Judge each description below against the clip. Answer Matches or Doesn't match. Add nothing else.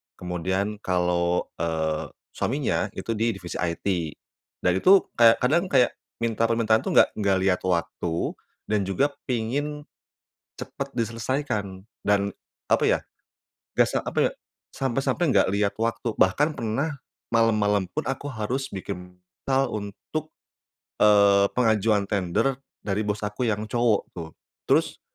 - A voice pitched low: Matches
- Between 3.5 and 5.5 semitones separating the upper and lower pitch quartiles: Matches